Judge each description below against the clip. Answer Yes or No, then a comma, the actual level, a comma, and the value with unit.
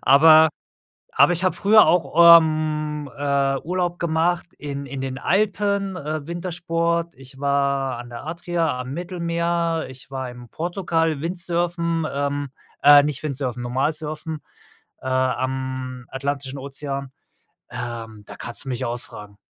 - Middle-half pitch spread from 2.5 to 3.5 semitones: No, average, 4.2 semitones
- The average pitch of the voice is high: No, medium, 150 Hz